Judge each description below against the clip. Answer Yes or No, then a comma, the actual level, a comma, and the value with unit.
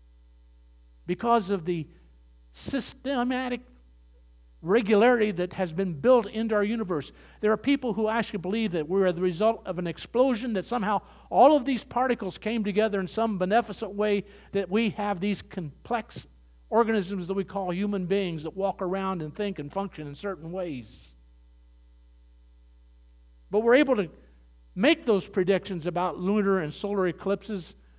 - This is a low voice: No, high, 195 Hz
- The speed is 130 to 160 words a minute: Yes, average, 150 wpm